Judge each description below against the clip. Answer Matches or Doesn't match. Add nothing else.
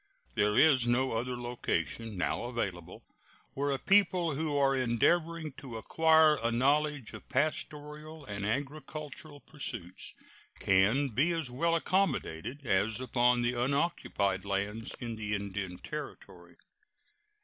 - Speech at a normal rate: Doesn't match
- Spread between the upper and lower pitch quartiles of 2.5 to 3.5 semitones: Doesn't match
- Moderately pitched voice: Doesn't match